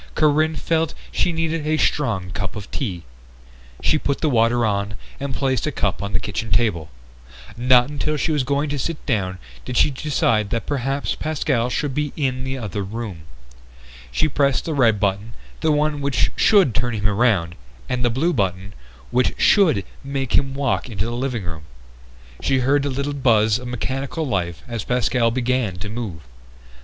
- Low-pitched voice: Yes, low, 125 Hz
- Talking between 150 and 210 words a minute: Yes, average, 180 wpm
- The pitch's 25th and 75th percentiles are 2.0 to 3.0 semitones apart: No, average, 5.2 semitones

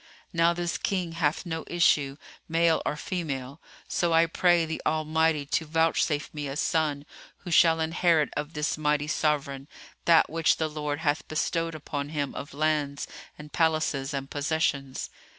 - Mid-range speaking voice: Yes, medium, 155 Hz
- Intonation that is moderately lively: No, narrow, 2.1 semitones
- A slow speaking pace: No, average, 155 wpm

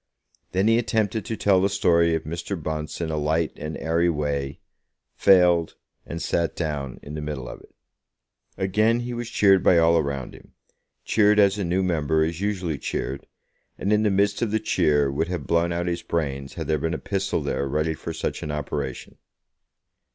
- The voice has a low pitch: Yes, very low, 85 Hz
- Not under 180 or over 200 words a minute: Yes, average, 195 wpm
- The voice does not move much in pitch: No, average, 4.3 semitones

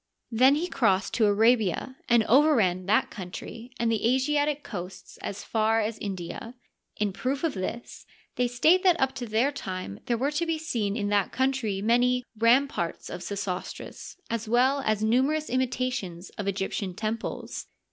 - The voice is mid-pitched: No, high, 230 Hz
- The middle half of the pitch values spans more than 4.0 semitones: Yes, average, 4.4 semitones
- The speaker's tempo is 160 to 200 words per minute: Yes, average, 165 wpm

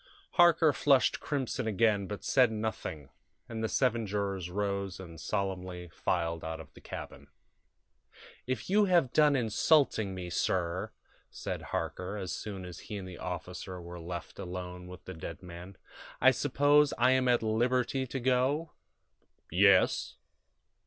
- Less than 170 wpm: Yes, average, 145 wpm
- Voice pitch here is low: Yes, low, 100 Hz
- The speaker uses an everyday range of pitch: No, wide, 6.0 semitones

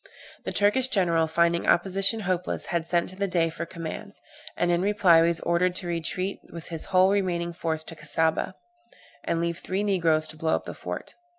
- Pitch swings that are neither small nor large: No, narrow, 2.2 semitones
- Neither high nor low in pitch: Yes, medium, 170 Hz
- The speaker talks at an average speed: Yes, average, 195 wpm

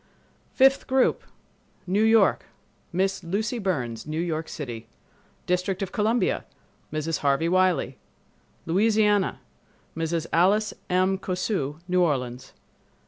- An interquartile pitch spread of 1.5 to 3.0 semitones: No, average, 4.7 semitones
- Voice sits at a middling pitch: Yes, medium, 180 Hz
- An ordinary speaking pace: No, slow, 90 wpm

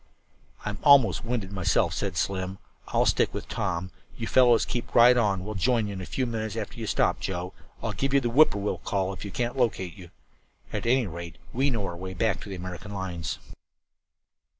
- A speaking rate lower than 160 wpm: No, fast, 205 wpm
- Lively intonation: No, average, 4.1 semitones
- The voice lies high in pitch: No, low, 100 Hz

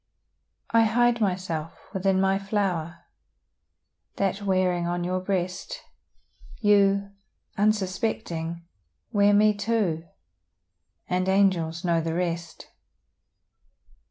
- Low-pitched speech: No, high, 190 Hz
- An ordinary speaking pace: No, slow, 90 wpm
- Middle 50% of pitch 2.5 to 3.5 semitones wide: Yes, average, 2.9 semitones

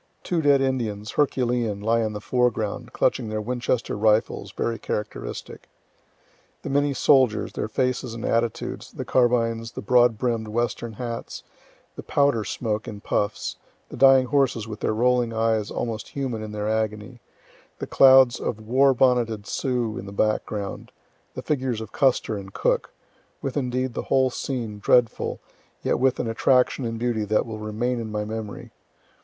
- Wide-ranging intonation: No, average, 2.9 semitones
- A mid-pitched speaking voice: No, low, 115 Hz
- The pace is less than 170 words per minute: Yes, average, 160 wpm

